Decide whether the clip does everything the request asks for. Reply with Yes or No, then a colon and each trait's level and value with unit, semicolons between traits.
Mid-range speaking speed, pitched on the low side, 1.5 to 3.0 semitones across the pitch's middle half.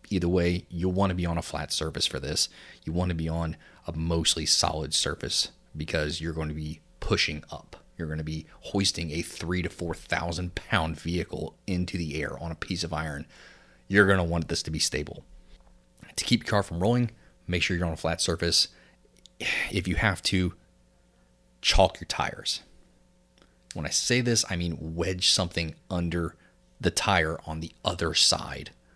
Yes: average, 190 wpm; very low, 85 Hz; narrow, 2.5 semitones